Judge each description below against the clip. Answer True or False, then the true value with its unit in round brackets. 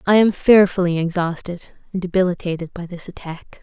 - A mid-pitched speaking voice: True (180 Hz)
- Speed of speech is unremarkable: True (150 wpm)